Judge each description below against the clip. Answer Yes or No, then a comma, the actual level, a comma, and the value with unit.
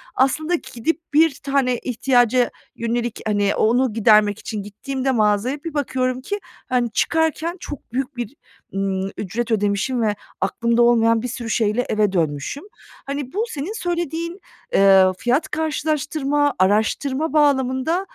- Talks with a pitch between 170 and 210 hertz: No, very high, 250 Hz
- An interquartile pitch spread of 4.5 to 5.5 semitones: Yes, average, 5.1 semitones